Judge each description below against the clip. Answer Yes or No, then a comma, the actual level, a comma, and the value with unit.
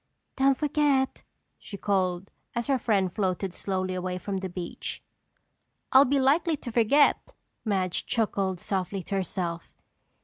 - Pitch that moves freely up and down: Yes, wide, 6.1 semitones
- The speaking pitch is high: Yes, high, 200 Hz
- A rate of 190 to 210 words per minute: No, slow, 135 wpm